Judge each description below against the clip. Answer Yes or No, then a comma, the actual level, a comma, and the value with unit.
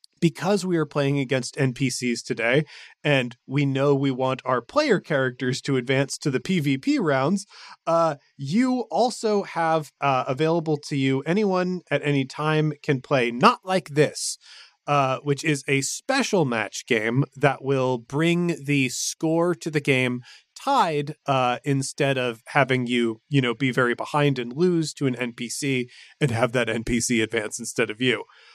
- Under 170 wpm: Yes, average, 160 wpm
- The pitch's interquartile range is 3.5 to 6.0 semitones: Yes, average, 3.9 semitones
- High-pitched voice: No, medium, 140 Hz